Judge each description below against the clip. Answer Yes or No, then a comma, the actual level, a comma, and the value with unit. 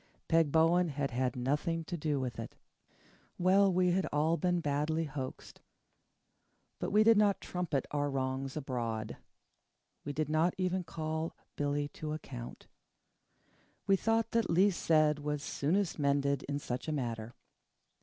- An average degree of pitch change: Yes, average, 4.0 semitones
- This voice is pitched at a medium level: Yes, medium, 155 Hz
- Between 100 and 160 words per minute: Yes, average, 145 wpm